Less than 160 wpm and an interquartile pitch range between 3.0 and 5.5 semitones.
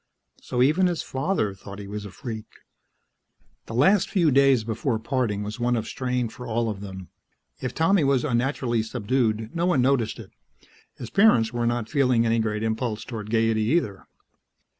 No: average, 175 wpm; average, 3.6 semitones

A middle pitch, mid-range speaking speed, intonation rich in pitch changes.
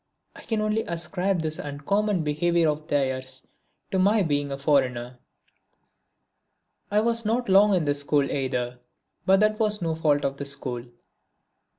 Yes: medium, 155 Hz; average, 160 wpm; wide, 6.1 semitones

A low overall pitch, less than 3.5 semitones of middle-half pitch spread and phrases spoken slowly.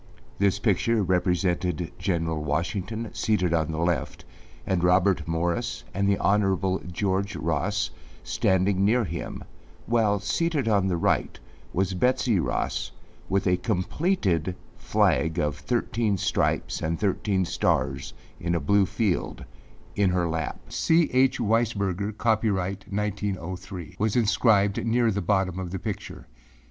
Yes: very low, 95 Hz; average, 3.1 semitones; slow, 130 wpm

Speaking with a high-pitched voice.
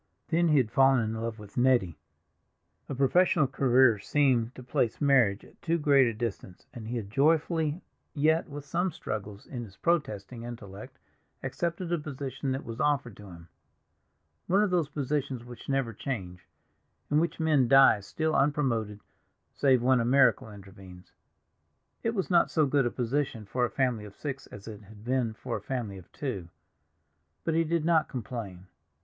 No: low, 130 Hz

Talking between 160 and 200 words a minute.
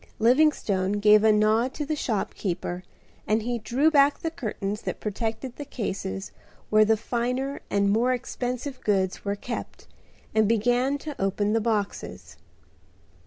No: average, 145 wpm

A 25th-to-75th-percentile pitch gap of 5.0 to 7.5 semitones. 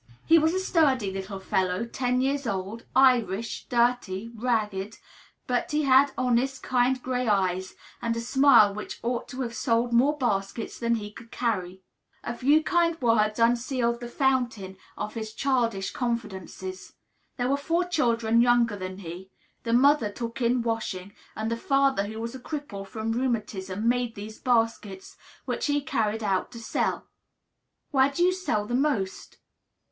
No: average, 3.7 semitones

